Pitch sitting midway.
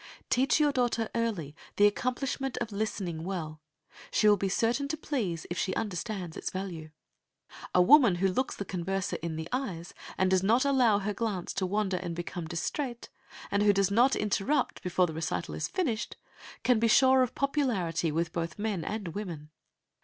No: high, 200 Hz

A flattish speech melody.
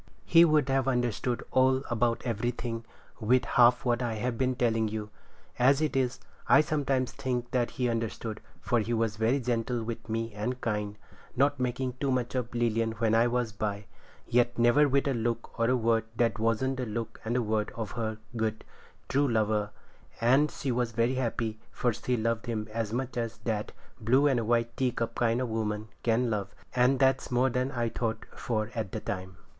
Yes: narrow, 2.2 semitones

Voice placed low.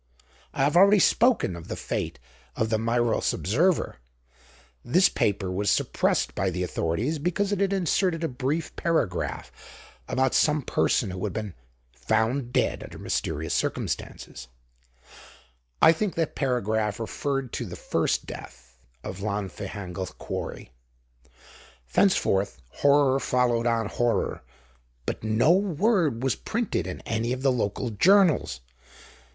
Yes: low, 120 Hz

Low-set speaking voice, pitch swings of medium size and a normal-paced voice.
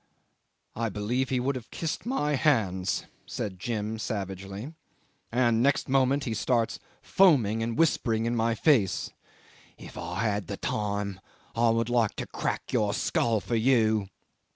Yes: low, 115 Hz; average, 3.6 semitones; average, 150 wpm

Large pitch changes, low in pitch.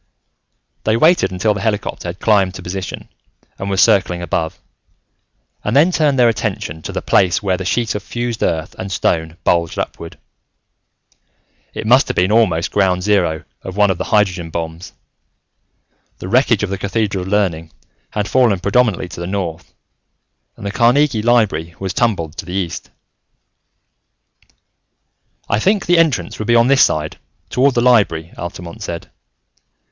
No: average, 4.9 semitones; low, 100 Hz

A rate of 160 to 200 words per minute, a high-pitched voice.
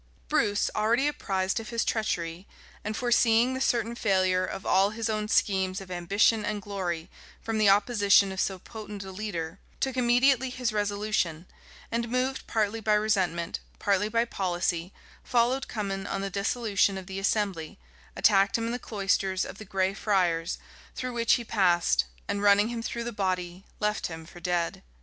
Yes: average, 175 wpm; high, 205 Hz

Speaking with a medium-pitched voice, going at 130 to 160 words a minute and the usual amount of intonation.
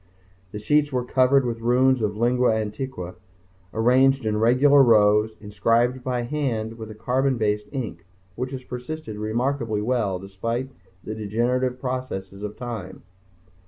No: low, 120 Hz; average, 140 wpm; average, 3.3 semitones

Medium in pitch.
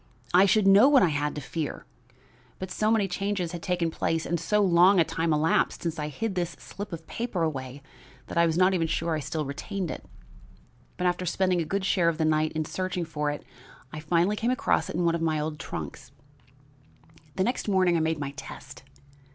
Yes: medium, 170 Hz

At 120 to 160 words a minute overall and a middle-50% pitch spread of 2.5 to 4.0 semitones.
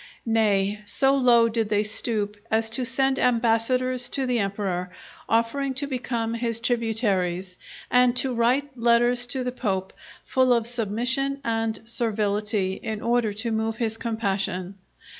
Yes: average, 140 wpm; average, 2.8 semitones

